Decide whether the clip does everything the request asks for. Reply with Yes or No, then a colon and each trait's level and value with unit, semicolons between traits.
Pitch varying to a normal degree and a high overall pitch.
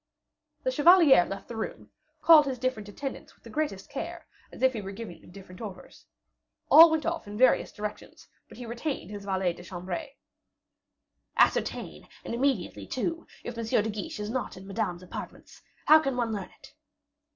No: wide, 5.7 semitones; high, 225 Hz